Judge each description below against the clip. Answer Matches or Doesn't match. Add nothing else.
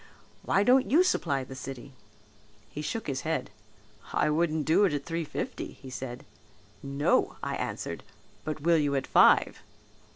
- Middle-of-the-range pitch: Matches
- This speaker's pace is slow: Doesn't match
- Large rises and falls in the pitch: Doesn't match